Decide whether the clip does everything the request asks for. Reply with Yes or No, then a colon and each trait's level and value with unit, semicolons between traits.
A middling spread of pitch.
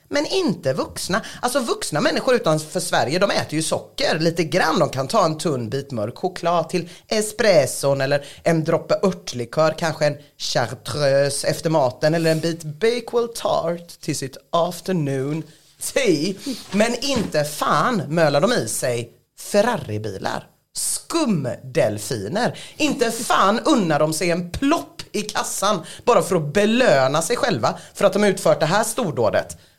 No: wide, 6.0 semitones